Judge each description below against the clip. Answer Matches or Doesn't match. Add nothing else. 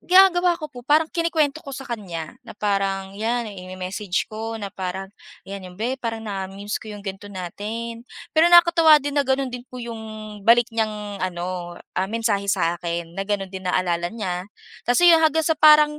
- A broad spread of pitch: Matches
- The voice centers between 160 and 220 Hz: Matches